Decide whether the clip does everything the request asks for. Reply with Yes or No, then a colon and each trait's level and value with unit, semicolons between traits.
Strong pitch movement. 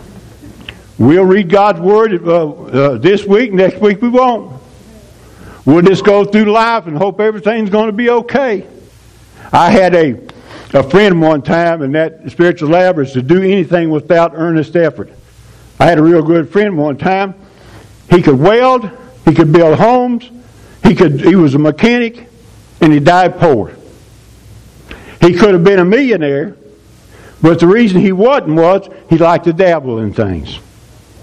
Yes: wide, 6.5 semitones